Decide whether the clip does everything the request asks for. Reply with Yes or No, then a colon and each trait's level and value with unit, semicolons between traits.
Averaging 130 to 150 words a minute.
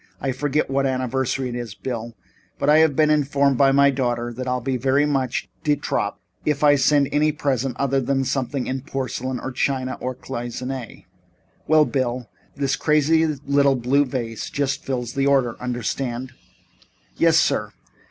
No: average, 170 wpm